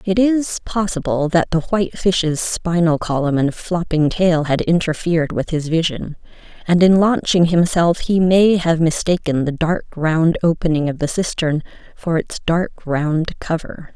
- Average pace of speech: Yes, average, 160 wpm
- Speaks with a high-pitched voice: No, medium, 170 Hz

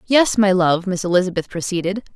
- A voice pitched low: No, high, 190 Hz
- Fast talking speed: No, average, 165 wpm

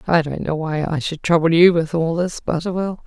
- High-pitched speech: No, medium, 165 Hz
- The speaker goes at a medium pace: No, fast, 235 wpm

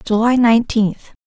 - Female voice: Yes, female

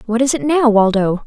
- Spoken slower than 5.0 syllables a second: No, 5.4 syllables/s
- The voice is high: Yes, high, 230 Hz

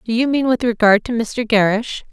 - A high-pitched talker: Yes, high, 230 Hz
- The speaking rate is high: Yes, fast, 225 wpm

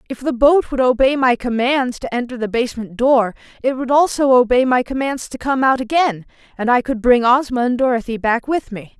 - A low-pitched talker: No, very high, 250 Hz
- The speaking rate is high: Yes, fast, 215 wpm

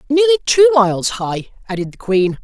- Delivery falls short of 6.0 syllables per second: Yes, 5.5 syllables/s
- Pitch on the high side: Yes, high, 245 Hz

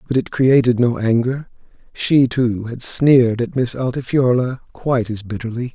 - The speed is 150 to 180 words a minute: Yes, average, 155 wpm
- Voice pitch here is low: Yes, low, 125 Hz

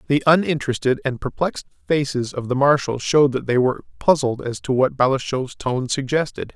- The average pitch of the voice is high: No, low, 135 Hz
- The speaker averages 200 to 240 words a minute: No, average, 175 wpm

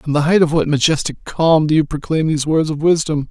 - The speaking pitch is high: No, medium, 155 Hz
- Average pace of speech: No, fast, 255 wpm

